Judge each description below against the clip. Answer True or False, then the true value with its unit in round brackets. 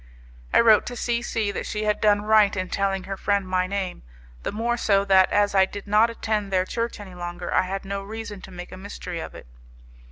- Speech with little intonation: True (2.2 semitones)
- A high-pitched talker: True (200 Hz)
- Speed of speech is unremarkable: False (230 wpm)